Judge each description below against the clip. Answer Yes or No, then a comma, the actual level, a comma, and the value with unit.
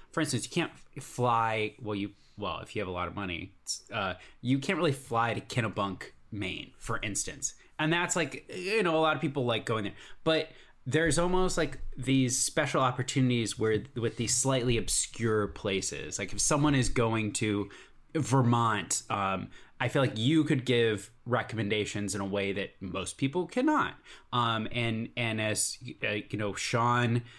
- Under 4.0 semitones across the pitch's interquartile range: No, average, 4.9 semitones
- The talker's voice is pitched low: Yes, low, 120 Hz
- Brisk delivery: No, average, 175 wpm